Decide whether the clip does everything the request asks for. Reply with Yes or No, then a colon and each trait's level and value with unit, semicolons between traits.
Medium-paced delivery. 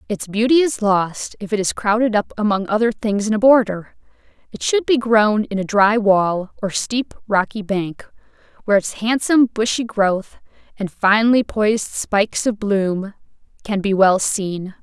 Yes: average, 170 wpm